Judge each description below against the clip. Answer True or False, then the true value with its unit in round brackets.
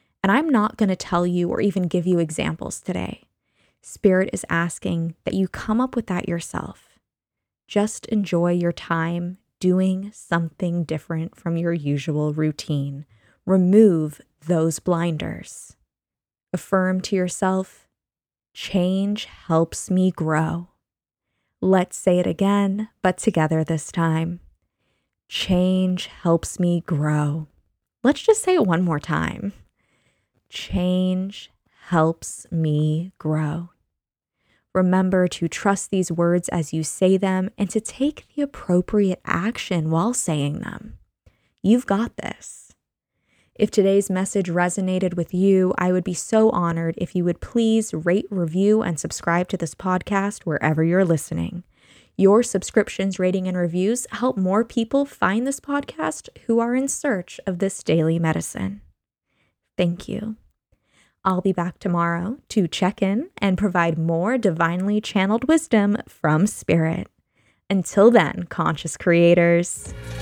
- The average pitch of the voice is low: False (185 Hz)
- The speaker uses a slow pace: True (130 wpm)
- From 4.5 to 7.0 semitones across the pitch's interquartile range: False (3.2 semitones)